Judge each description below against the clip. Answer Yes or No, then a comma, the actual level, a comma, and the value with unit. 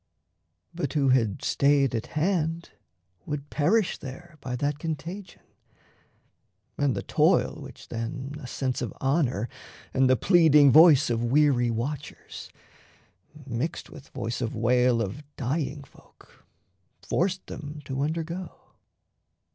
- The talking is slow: Yes, slow, 125 wpm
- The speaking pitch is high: No, medium, 140 Hz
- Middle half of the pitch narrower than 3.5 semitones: No, average, 3.8 semitones